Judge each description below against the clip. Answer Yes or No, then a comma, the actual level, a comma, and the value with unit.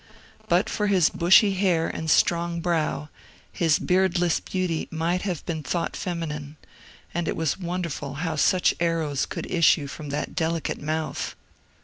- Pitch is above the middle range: No, medium, 170 Hz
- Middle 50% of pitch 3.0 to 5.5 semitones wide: No, narrow, 2.4 semitones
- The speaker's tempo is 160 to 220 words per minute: No, average, 150 wpm